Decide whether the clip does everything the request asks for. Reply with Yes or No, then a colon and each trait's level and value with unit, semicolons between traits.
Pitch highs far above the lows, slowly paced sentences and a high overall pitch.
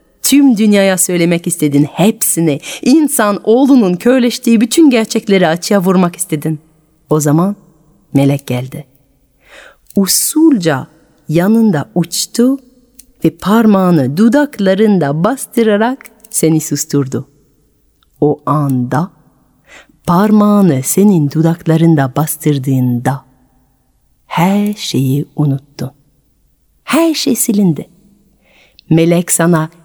No: wide, 6.3 semitones; slow, 80 wpm; medium, 175 Hz